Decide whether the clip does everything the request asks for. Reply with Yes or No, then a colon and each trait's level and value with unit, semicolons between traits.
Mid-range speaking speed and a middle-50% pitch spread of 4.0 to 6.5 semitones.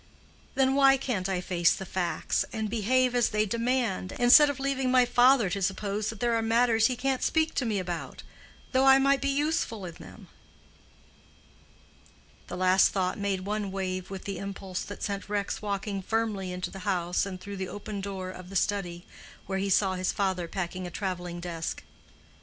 Yes: average, 185 wpm; average, 4.6 semitones